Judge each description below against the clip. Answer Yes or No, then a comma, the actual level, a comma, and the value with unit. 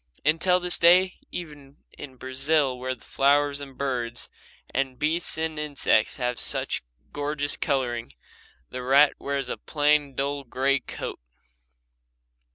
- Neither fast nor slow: No, slow, 130 wpm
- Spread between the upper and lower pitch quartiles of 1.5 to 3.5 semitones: Yes, narrow, 2.6 semitones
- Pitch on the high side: No, medium, 140 Hz